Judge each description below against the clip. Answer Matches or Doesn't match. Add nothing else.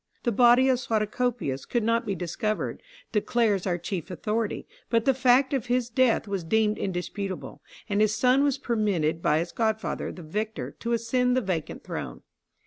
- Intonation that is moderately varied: Matches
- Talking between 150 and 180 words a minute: Matches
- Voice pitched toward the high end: Matches